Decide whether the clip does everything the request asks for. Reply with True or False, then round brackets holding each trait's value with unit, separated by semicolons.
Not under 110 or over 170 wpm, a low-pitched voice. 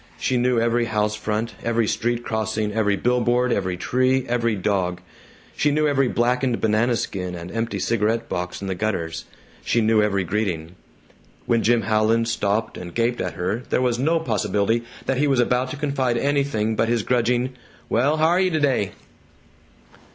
True (165 wpm; 115 Hz)